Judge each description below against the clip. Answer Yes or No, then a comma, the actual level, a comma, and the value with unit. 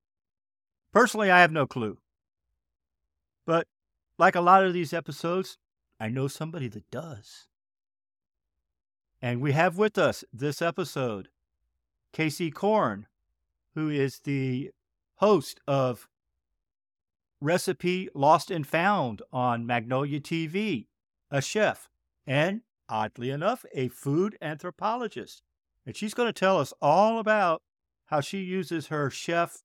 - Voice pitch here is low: No, medium, 145 Hz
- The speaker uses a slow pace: Yes, slow, 120 wpm